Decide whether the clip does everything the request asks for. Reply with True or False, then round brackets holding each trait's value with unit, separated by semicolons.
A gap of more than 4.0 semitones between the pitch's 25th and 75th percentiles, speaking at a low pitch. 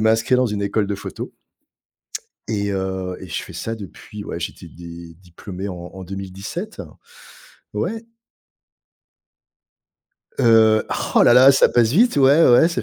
True (4.9 semitones; 105 Hz)